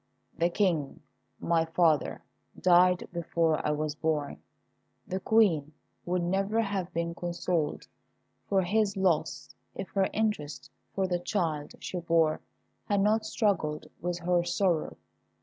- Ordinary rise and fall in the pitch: Yes, average, 3.1 semitones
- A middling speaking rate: No, slow, 130 wpm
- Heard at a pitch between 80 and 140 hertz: No, medium, 175 Hz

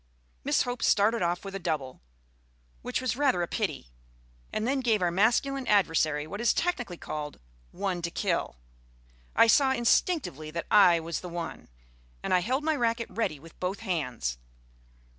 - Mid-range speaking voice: No, high, 195 Hz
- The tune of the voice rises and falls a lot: Yes, wide, 6.2 semitones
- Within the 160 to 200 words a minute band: Yes, average, 165 wpm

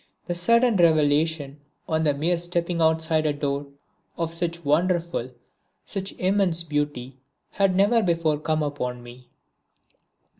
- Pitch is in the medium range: Yes, medium, 160 Hz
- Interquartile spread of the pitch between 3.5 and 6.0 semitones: No, average, 3.1 semitones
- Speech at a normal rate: No, slow, 125 wpm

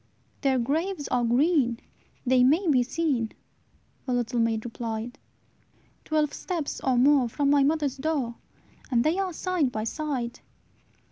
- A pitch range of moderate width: Yes, average, 4.3 semitones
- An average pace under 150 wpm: Yes, average, 140 wpm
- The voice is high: Yes, very high, 265 Hz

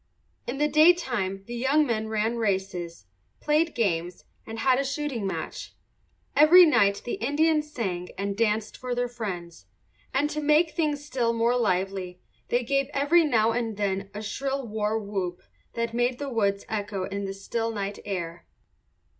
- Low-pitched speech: No, high, 230 Hz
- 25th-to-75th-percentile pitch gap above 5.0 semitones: Yes, wide, 5.6 semitones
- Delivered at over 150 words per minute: Yes, average, 165 wpm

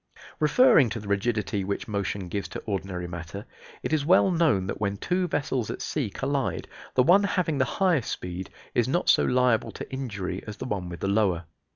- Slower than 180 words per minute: No, average, 200 wpm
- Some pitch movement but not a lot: No, wide, 6.7 semitones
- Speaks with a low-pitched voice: Yes, low, 110 Hz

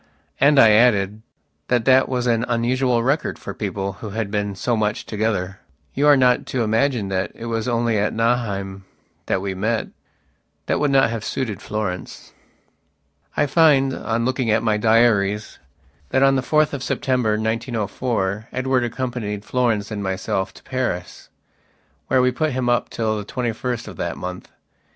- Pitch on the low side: Yes, low, 115 Hz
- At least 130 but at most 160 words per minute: No, average, 170 wpm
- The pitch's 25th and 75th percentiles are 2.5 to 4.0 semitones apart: Yes, average, 3.5 semitones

